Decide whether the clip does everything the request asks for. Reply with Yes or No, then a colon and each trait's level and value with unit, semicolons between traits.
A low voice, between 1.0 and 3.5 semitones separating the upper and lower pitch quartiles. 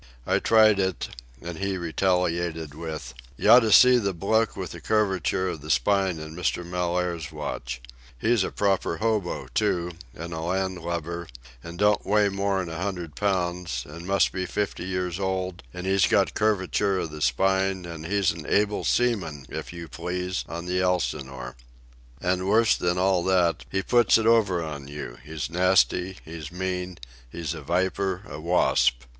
Yes: very low, 90 Hz; narrow, 2.5 semitones